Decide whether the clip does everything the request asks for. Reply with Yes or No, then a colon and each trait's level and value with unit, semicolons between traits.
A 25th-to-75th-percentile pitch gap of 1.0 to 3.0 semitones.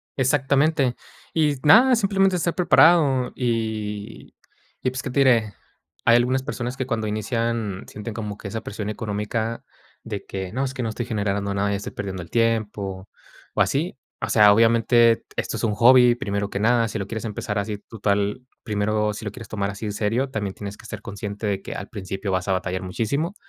No: average, 3.6 semitones